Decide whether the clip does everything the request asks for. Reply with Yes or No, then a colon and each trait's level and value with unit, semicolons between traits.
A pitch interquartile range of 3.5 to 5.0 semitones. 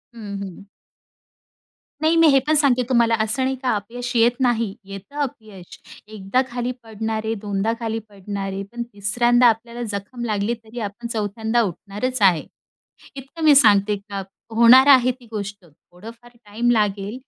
No: average, 3.1 semitones